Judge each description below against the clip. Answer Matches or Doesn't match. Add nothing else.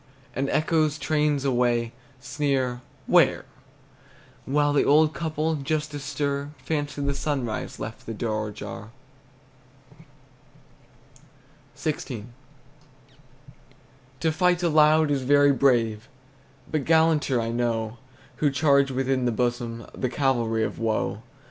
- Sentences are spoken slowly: Matches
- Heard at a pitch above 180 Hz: Doesn't match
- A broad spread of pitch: Doesn't match